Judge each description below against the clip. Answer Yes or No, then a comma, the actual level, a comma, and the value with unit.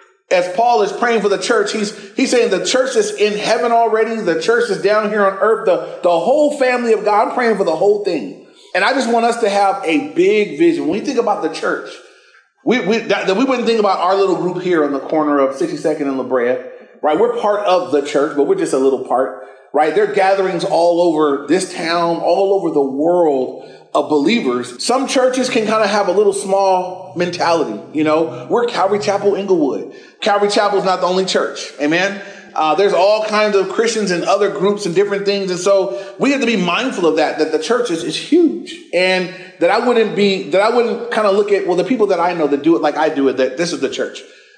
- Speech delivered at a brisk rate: Yes, fast, 240 wpm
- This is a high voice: Yes, high, 200 Hz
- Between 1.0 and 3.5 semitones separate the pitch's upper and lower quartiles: No, average, 5.3 semitones